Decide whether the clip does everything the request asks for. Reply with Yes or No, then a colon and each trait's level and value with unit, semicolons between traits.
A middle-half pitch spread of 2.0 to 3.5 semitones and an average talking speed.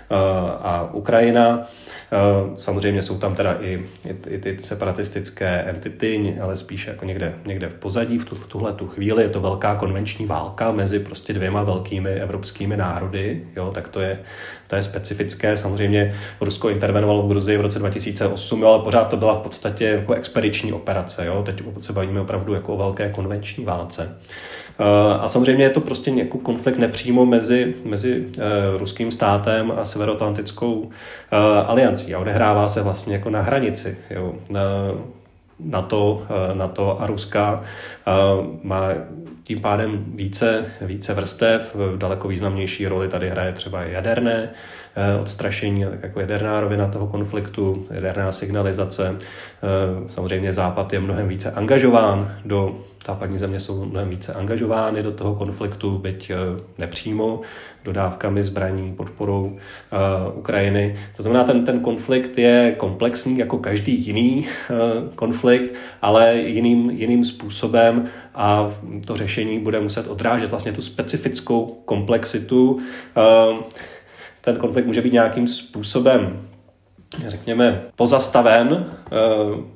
Yes: average, 2.7 semitones; average, 135 wpm